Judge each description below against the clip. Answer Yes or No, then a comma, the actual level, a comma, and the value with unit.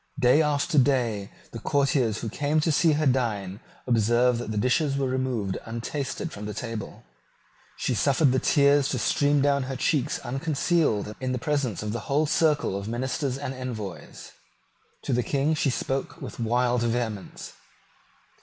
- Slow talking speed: No, average, 165 wpm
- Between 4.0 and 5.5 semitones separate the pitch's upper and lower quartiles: No, average, 3.6 semitones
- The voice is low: Yes, low, 130 Hz